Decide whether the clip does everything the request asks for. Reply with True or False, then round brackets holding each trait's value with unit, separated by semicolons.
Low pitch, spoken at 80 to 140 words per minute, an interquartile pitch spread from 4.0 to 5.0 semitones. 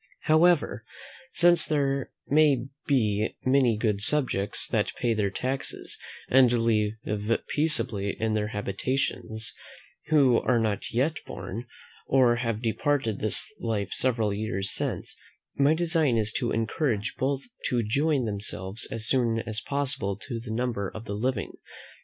True (115 Hz; 135 wpm; 4.3 semitones)